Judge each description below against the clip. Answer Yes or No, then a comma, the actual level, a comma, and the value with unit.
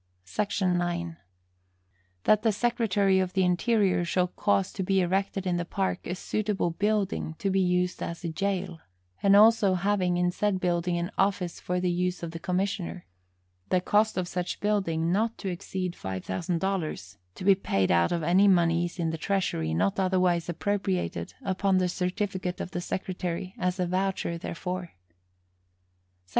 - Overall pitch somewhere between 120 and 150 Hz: No, medium, 180 Hz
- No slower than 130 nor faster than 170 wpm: Yes, average, 165 wpm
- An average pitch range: No, narrow, 2.1 semitones